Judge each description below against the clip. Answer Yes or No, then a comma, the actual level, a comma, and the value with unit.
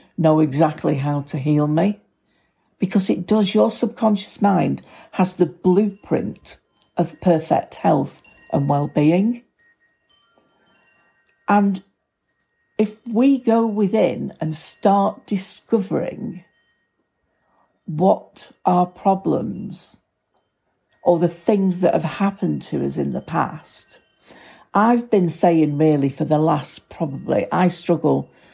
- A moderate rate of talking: No, slow, 110 wpm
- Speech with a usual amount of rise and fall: Yes, average, 4.8 semitones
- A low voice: No, medium, 185 Hz